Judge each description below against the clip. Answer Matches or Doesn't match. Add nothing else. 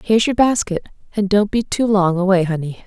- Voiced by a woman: Matches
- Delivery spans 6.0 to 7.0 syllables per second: Doesn't match